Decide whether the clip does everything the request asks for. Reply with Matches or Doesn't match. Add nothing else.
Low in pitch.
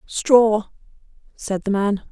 Doesn't match